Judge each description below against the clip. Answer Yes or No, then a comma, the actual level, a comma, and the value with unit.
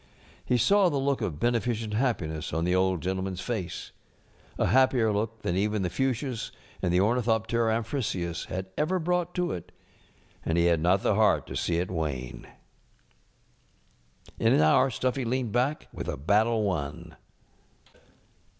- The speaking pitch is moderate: No, low, 105 Hz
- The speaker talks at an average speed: Yes, average, 165 wpm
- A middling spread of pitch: No, wide, 6.0 semitones